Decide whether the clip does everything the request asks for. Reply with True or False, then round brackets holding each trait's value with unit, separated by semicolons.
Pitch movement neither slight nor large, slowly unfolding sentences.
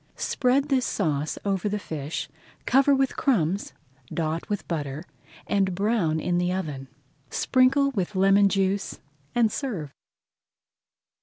False (6.7 semitones; 125 wpm)